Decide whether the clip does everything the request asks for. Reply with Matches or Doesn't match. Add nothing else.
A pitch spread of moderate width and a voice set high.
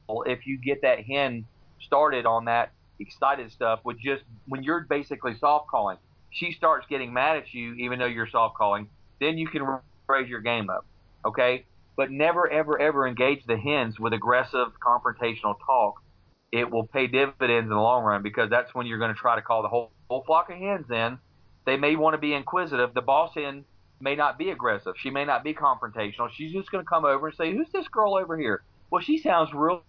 Doesn't match